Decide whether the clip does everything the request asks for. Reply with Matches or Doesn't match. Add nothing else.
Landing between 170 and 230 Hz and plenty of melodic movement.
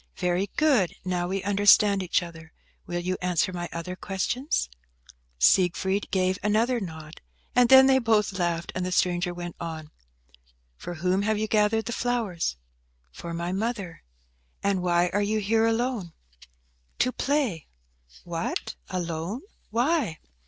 Doesn't match